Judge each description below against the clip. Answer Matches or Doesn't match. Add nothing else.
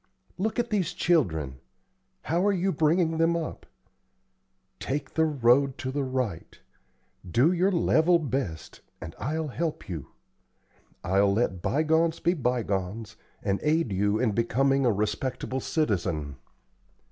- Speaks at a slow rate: Matches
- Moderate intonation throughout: Doesn't match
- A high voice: Doesn't match